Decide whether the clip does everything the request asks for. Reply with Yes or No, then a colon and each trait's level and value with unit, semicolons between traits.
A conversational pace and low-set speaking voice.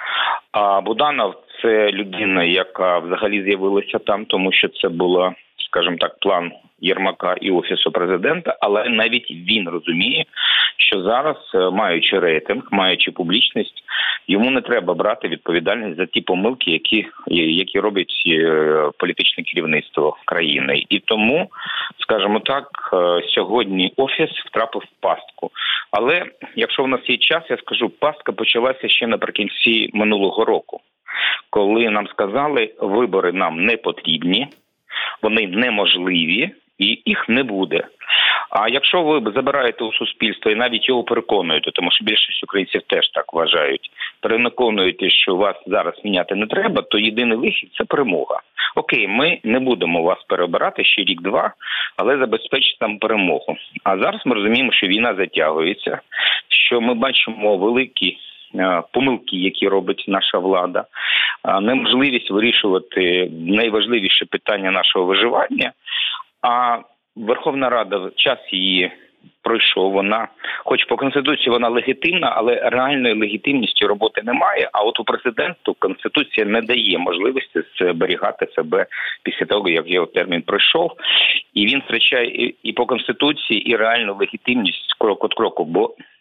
Yes: average, 130 wpm; low, 110 Hz